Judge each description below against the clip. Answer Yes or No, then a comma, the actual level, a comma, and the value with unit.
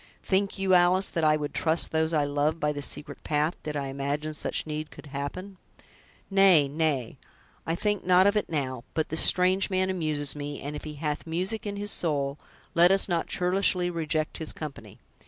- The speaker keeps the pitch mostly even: No, average, 3.8 semitones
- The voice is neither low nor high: Yes, medium, 160 Hz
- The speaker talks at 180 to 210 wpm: Yes, average, 195 wpm